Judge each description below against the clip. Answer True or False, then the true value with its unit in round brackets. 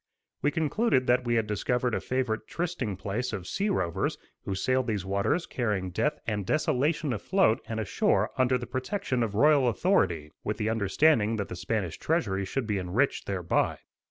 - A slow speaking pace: False (175 wpm)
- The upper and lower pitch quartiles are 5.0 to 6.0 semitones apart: True (5.5 semitones)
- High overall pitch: False (115 Hz)